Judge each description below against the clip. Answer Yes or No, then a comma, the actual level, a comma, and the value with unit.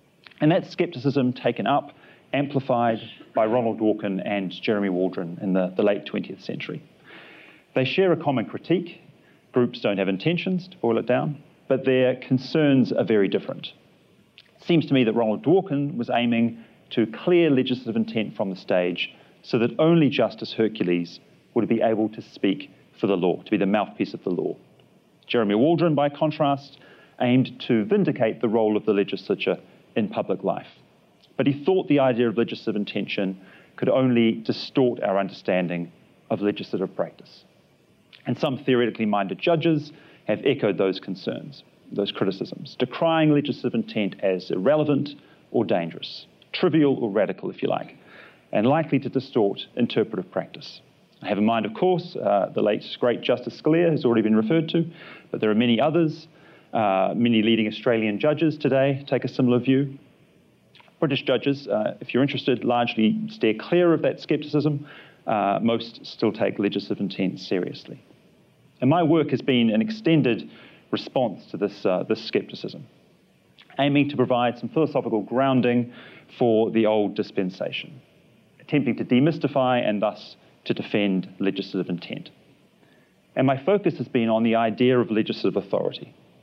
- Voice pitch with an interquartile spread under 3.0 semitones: No, average, 5.0 semitones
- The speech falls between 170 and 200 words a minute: No, average, 160 wpm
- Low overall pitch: Yes, low, 125 Hz